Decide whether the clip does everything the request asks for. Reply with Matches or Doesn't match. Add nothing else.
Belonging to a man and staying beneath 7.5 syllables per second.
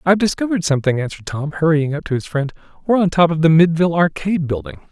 Doesn't match